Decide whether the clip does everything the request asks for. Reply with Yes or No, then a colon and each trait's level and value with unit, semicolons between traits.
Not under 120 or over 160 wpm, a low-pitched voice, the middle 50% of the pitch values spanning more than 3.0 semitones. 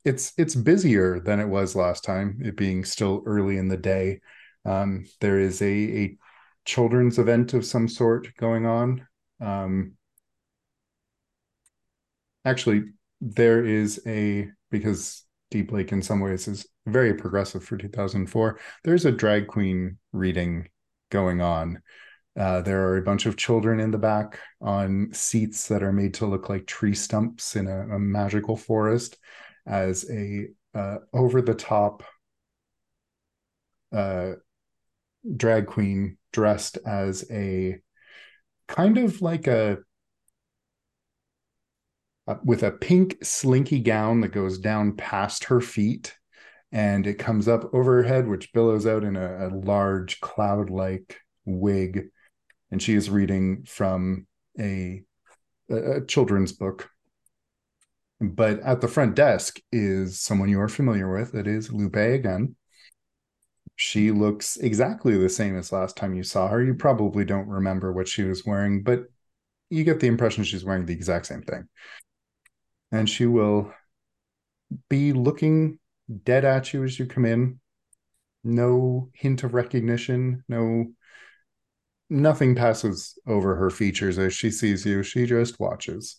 Yes: average, 140 wpm; low, 105 Hz; average, 3.5 semitones